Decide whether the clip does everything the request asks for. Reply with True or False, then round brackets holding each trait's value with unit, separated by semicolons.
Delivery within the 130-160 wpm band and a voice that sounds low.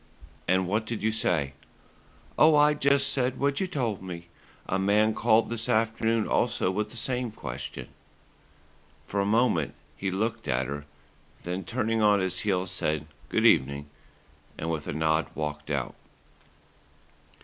True (150 wpm; 105 Hz)